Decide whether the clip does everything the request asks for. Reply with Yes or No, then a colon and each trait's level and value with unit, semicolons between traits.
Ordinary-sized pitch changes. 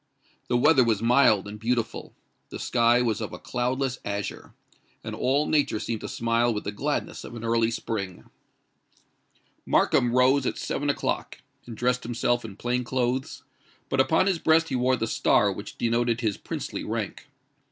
No: narrow, 2.1 semitones